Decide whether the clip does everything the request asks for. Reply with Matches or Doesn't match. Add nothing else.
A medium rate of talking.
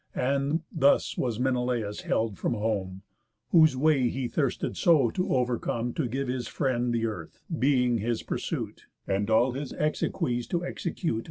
Matches